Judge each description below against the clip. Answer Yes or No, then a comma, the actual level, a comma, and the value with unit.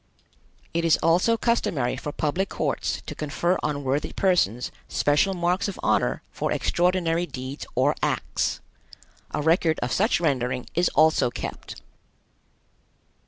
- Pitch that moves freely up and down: No, average, 4.1 semitones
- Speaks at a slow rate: Yes, slow, 130 wpm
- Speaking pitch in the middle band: Yes, medium, 160 Hz